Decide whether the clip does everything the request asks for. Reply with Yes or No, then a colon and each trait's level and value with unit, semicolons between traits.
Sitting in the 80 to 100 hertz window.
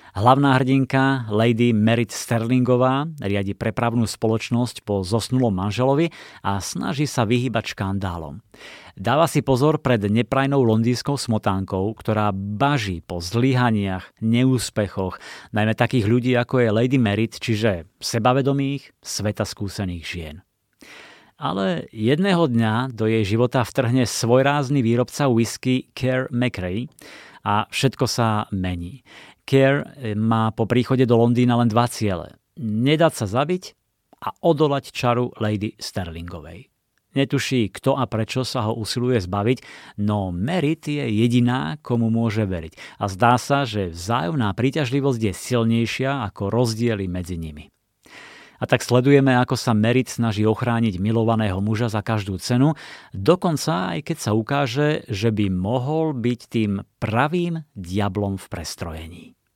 No: low, 115 Hz